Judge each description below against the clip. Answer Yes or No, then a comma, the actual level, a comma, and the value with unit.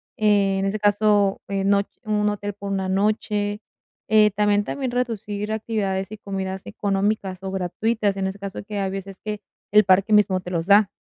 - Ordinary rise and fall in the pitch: No, narrow, 1.4 semitones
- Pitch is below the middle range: No, high, 205 Hz